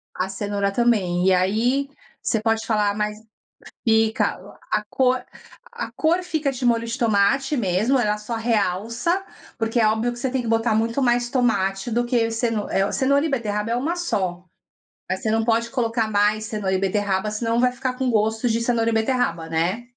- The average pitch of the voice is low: No, high, 225 Hz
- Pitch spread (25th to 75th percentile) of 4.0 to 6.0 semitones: No, average, 2.9 semitones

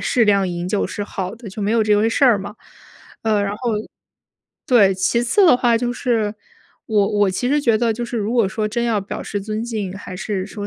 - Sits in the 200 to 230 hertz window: Yes, high, 215 Hz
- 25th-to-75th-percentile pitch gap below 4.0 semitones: Yes, average, 2.8 semitones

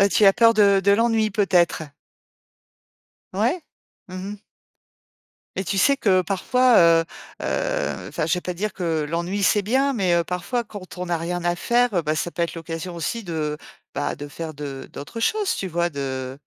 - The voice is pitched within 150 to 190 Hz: Yes, medium, 185 Hz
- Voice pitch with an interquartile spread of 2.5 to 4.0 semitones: No, average, 4.5 semitones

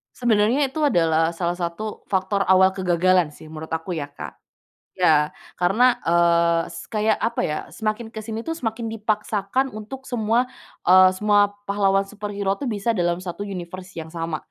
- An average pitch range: Yes, average, 4.1 semitones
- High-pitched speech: Yes, high, 195 Hz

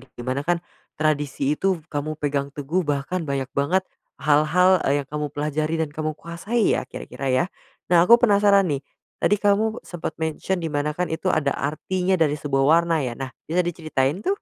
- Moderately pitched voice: Yes, medium, 155 Hz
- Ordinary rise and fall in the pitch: Yes, average, 3.9 semitones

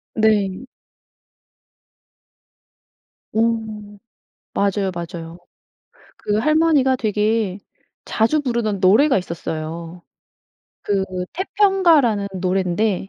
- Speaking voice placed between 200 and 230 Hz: Yes, high, 210 Hz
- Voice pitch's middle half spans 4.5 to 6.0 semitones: Yes, average, 5.3 semitones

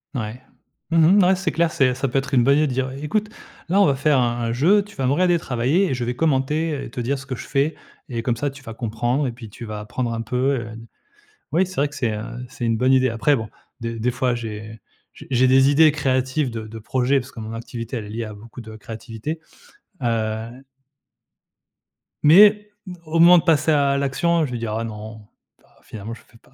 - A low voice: Yes, low, 130 Hz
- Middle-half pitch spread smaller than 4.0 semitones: No, average, 4.5 semitones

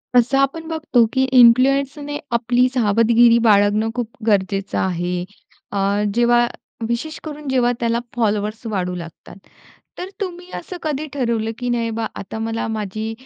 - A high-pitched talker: Yes, high, 235 Hz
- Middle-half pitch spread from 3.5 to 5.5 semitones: Yes, average, 3.9 semitones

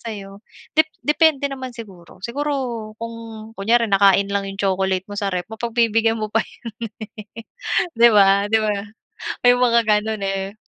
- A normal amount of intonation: Yes, average, 3.0 semitones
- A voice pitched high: Yes, high, 215 Hz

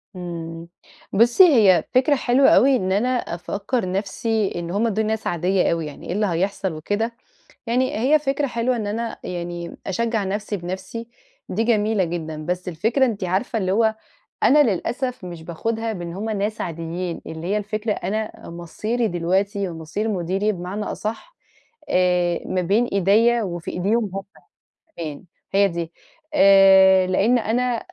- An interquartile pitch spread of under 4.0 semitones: No, average, 4.3 semitones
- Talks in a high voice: Yes, high, 200 Hz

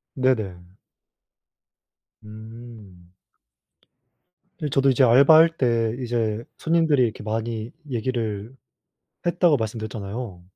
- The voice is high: No, low, 115 Hz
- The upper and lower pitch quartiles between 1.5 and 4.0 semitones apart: Yes, average, 3.3 semitones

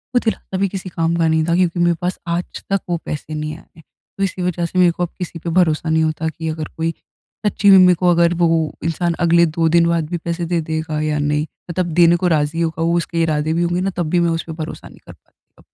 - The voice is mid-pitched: Yes, medium, 170 Hz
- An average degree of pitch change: No, narrow, 1.7 semitones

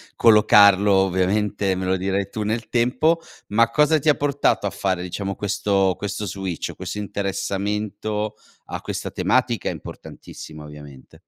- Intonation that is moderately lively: No, narrow, 2.2 semitones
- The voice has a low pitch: Yes, low, 100 Hz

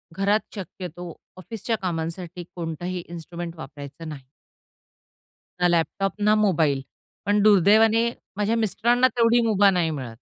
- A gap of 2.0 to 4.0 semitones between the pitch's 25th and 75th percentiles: No, average, 4.4 semitones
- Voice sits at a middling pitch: Yes, medium, 180 Hz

